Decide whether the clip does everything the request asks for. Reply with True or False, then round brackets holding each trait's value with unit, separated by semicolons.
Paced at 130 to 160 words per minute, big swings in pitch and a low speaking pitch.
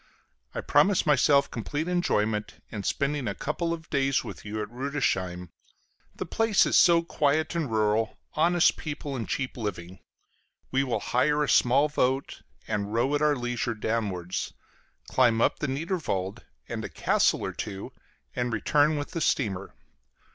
True (155 wpm; 5.8 semitones; 130 Hz)